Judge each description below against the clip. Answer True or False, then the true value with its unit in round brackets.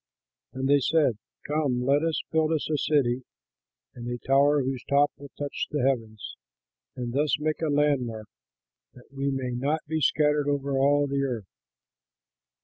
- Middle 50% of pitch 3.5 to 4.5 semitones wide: False (2.7 semitones)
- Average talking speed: True (160 wpm)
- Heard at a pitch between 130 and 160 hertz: True (140 Hz)